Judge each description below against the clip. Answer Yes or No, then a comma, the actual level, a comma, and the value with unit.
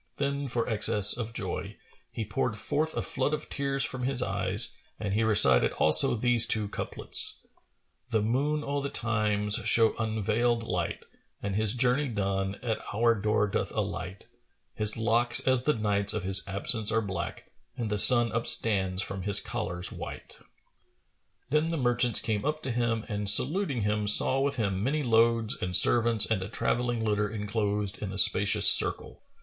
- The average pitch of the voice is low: Yes, low, 110 Hz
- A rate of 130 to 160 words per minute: No, average, 175 wpm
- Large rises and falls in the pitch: No, average, 3.0 semitones